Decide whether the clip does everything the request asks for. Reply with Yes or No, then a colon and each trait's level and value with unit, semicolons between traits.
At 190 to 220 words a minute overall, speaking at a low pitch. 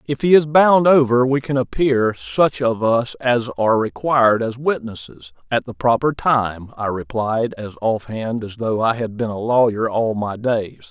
Yes: average, 195 wpm; low, 120 Hz